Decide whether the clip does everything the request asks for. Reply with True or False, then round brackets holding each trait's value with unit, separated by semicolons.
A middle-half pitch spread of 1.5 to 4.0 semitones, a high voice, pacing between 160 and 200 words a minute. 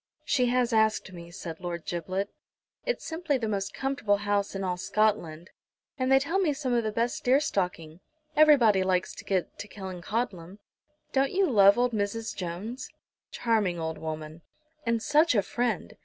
False (5.6 semitones; 210 Hz; 170 wpm)